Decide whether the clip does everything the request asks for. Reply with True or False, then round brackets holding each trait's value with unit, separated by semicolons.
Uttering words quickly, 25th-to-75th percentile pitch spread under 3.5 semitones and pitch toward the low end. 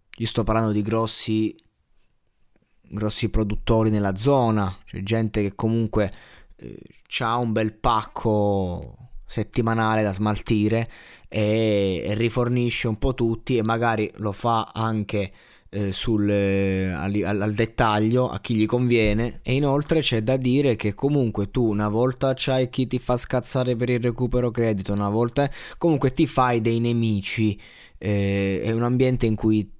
False (150 wpm; 2.8 semitones; 110 Hz)